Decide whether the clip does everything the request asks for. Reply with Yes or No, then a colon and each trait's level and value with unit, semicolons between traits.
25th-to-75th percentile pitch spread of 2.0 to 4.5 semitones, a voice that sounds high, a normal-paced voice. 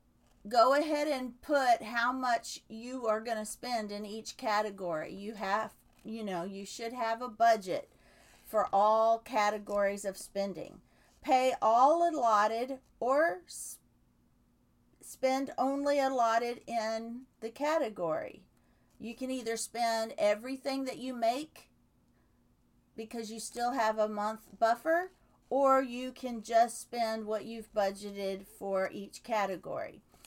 No: average, 3.4 semitones; high, 230 Hz; slow, 125 wpm